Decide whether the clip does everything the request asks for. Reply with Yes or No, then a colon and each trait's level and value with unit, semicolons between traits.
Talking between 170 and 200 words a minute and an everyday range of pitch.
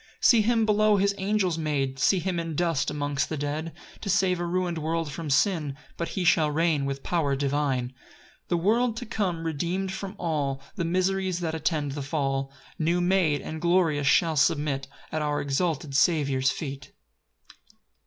Yes: average, 175 wpm; average, 4.1 semitones